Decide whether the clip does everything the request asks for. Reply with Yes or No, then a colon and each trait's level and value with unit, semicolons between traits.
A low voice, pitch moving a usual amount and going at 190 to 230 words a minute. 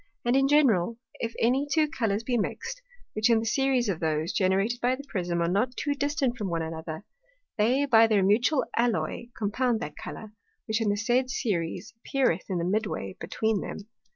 No: high, 225 Hz; average, 4.9 semitones; average, 200 wpm